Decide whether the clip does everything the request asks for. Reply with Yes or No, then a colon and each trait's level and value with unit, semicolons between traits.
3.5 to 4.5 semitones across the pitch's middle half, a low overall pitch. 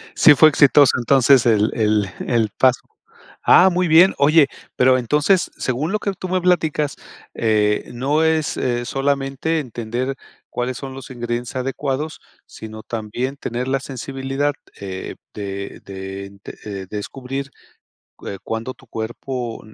Yes: average, 4.1 semitones; low, 130 Hz